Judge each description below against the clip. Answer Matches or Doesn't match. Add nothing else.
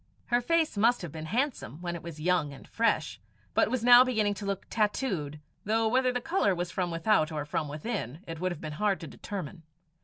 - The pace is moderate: Doesn't match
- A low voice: Doesn't match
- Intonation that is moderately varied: Doesn't match